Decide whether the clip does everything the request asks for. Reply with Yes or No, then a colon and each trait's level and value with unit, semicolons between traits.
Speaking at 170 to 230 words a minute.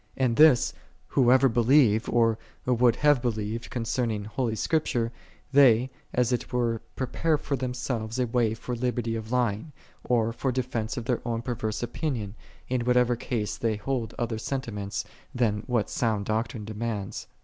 No: average, 155 wpm